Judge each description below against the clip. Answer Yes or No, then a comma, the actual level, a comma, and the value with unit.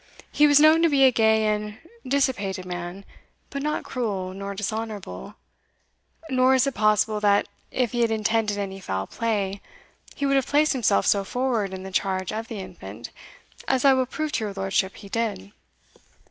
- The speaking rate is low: No, average, 180 wpm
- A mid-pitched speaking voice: No, high, 215 Hz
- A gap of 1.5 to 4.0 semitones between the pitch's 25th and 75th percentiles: No, average, 4.7 semitones